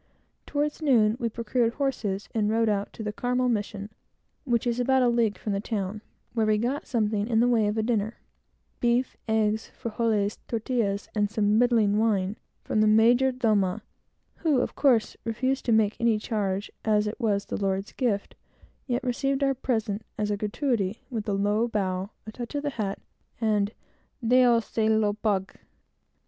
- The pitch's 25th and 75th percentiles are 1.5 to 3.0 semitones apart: Yes, narrow, 2.6 semitones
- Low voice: No, high, 220 Hz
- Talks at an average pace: Yes, average, 175 wpm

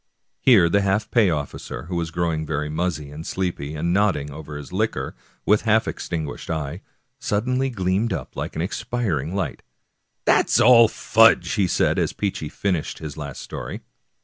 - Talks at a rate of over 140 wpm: Yes, average, 180 wpm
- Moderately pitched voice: No, very low, 90 Hz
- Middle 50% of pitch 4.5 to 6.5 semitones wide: Yes, average, 5.2 semitones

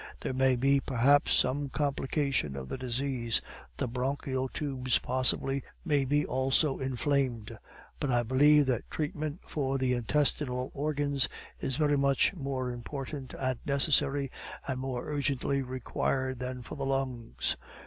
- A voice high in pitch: No, low, 135 Hz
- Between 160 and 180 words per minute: No, average, 140 wpm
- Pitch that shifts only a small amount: Yes, narrow, 1.9 semitones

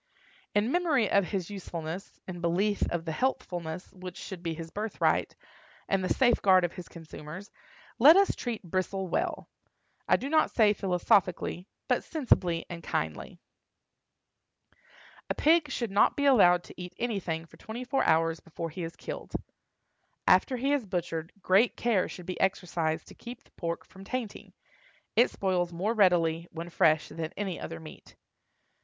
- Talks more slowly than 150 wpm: No, average, 160 wpm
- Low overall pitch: No, medium, 185 Hz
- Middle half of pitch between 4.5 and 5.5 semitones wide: Yes, average, 4.8 semitones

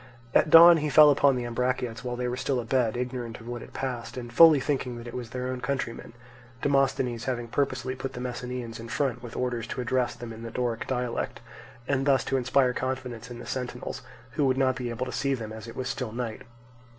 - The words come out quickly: Yes, fast, 225 wpm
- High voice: No, low, 125 Hz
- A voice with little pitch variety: Yes, narrow, 1.6 semitones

